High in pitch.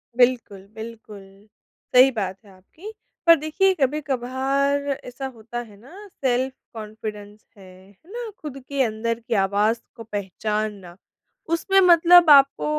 Yes: high, 240 Hz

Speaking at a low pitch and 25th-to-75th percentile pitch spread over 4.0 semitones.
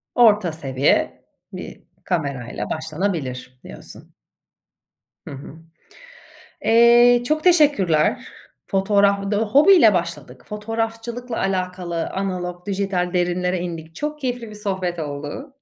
No: high, 190 Hz; average, 5.1 semitones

